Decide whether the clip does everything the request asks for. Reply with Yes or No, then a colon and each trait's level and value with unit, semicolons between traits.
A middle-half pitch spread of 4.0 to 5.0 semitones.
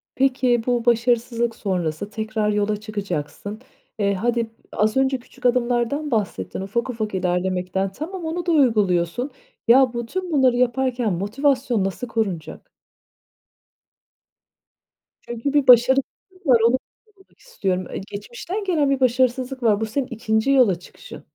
Yes: average, 4.3 semitones